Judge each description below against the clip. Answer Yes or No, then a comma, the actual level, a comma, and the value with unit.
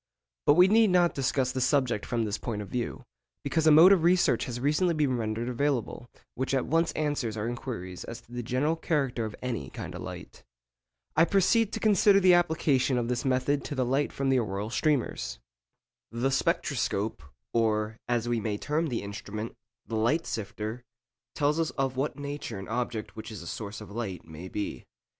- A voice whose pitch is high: No, low, 125 Hz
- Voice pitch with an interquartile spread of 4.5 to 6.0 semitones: Yes, average, 5.2 semitones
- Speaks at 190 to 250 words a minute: Yes, average, 195 wpm